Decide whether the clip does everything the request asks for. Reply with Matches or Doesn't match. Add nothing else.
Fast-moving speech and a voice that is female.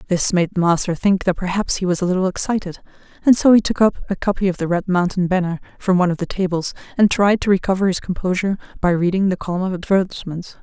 Matches